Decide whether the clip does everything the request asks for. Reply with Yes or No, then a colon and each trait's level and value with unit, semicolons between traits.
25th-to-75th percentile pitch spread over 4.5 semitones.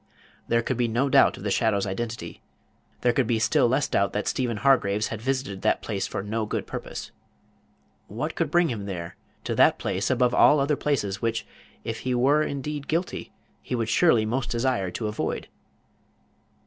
No: average, 4.0 semitones